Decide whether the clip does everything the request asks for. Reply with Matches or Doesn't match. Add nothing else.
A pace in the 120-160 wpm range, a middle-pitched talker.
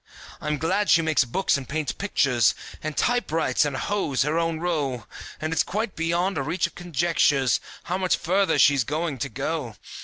Doesn't match